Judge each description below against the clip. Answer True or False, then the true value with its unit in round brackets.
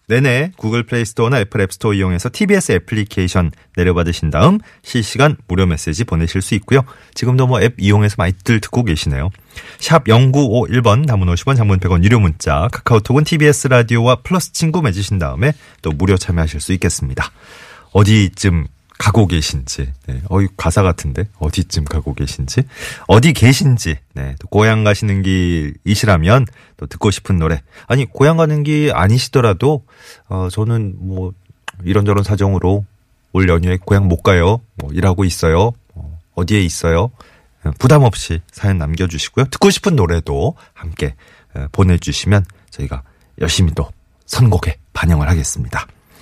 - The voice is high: False (100 Hz)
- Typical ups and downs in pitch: False (6.0 semitones)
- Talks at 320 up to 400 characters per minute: True (335 characters per minute)